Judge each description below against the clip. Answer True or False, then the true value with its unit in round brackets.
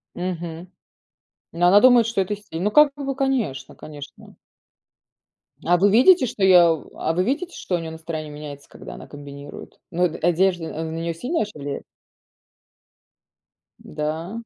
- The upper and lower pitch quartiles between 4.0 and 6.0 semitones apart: True (4.9 semitones)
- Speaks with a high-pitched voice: False (175 Hz)